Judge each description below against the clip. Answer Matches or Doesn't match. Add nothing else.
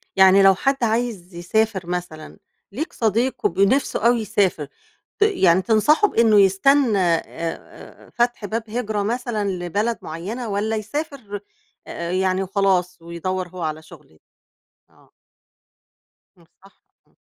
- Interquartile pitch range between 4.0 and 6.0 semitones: Matches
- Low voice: Doesn't match